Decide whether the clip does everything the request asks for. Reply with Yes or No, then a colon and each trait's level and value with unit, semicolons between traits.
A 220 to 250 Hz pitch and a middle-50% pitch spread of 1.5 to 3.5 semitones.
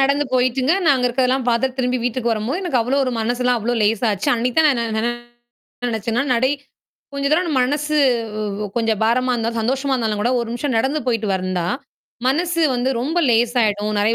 Yes: high, 245 Hz; average, 2.9 semitones